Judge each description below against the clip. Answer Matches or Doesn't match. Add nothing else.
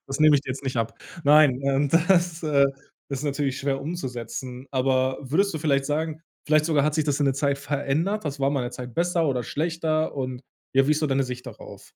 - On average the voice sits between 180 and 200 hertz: Doesn't match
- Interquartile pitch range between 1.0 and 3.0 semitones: Matches